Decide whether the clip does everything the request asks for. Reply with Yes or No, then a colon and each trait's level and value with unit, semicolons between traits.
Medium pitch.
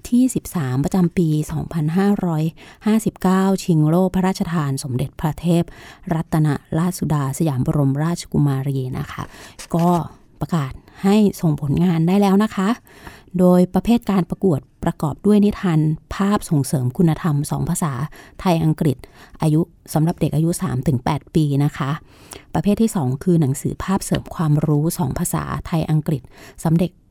Yes: medium, 165 Hz